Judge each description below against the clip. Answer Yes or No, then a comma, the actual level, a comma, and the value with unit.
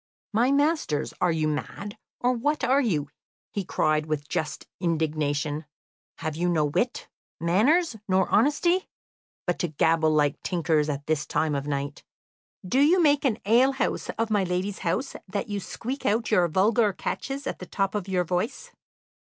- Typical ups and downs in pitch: No, wide, 7.5 semitones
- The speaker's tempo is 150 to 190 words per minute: Yes, average, 165 wpm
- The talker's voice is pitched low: No, medium, 185 Hz